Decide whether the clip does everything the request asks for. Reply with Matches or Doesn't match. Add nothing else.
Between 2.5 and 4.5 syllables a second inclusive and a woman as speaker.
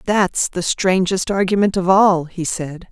Matches